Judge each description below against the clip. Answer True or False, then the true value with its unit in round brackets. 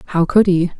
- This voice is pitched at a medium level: True (180 Hz)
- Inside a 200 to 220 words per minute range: False (230 wpm)